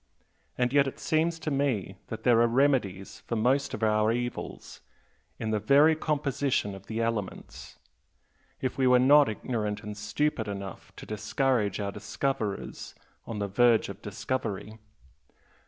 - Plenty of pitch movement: No, average, 4.4 semitones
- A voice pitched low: Yes, low, 115 Hz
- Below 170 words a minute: Yes, average, 150 wpm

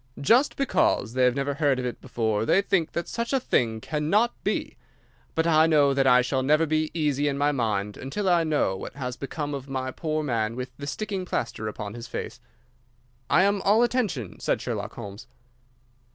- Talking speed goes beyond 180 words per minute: Yes, average, 195 wpm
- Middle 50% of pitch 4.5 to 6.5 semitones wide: Yes, average, 4.8 semitones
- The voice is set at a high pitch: No, medium, 140 Hz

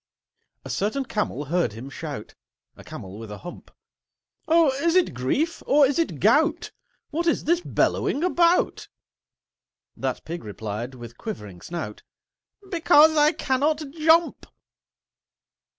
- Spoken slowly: Yes, slow, 130 wpm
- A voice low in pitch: No, very high, 260 Hz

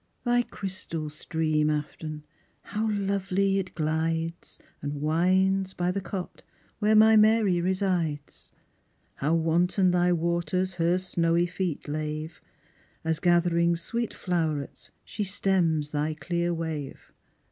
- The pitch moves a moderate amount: Yes, average, 3.0 semitones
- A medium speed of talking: No, slow, 115 wpm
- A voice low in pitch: No, medium, 175 Hz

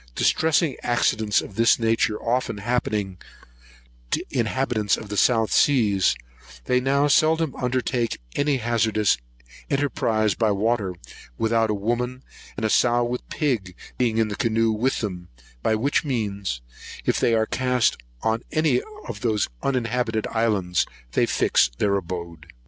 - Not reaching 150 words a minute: Yes, average, 140 wpm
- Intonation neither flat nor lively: Yes, average, 3.2 semitones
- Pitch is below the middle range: Yes, low, 115 Hz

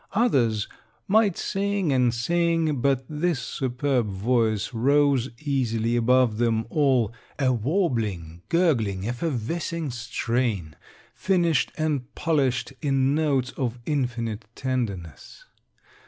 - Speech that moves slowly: Yes, slow, 100 wpm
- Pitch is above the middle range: No, low, 130 Hz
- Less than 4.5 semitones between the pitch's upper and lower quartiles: No, average, 4.8 semitones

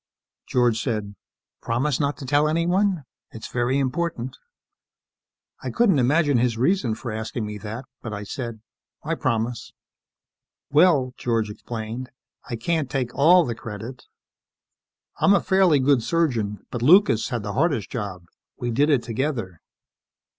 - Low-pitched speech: Yes, low, 125 Hz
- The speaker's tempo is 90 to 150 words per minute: Yes, average, 140 wpm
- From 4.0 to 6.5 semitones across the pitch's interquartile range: Yes, average, 5.0 semitones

